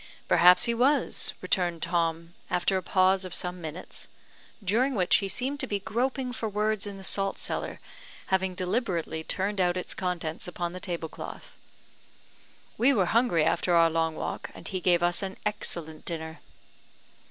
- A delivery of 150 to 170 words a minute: Yes, average, 165 wpm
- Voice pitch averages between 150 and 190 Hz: Yes, medium, 185 Hz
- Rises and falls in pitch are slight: No, average, 3.3 semitones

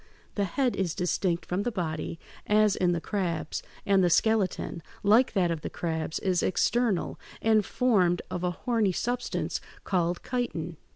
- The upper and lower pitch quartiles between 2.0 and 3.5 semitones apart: No, average, 3.9 semitones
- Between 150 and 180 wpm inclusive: Yes, average, 160 wpm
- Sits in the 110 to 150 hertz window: No, medium, 185 Hz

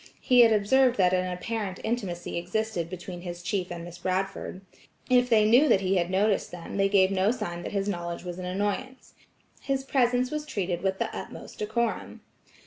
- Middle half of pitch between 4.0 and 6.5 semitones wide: Yes, average, 4.3 semitones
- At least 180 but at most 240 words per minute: Yes, average, 190 wpm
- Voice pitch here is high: Yes, high, 195 Hz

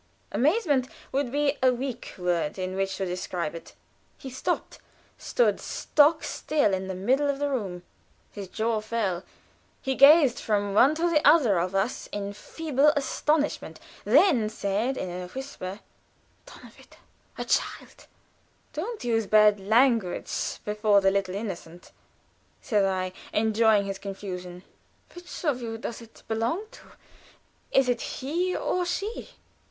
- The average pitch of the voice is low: No, high, 225 Hz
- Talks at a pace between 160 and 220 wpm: No, average, 140 wpm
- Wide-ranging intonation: Yes, wide, 6.4 semitones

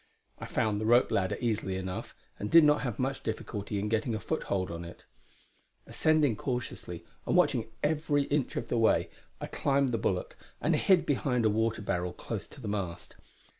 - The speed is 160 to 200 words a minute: Yes, average, 185 wpm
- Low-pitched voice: Yes, low, 115 Hz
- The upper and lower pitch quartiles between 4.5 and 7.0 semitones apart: Yes, average, 5.2 semitones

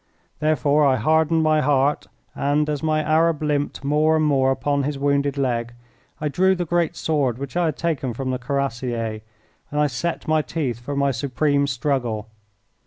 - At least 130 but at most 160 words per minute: No, average, 175 wpm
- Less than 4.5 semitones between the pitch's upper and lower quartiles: Yes, average, 2.8 semitones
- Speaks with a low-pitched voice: No, medium, 145 Hz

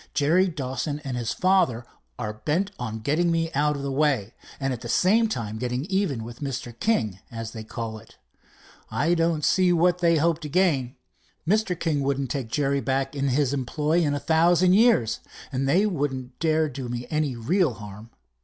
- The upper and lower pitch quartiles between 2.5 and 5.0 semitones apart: No, wide, 5.4 semitones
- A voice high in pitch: No, medium, 140 Hz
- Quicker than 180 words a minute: Yes, average, 190 wpm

